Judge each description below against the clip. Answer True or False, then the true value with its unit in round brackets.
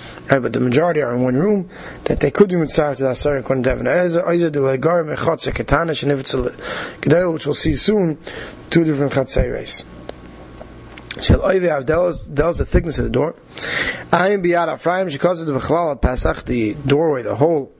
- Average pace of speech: False (210 wpm)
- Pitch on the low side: False (150 Hz)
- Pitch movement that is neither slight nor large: True (4.4 semitones)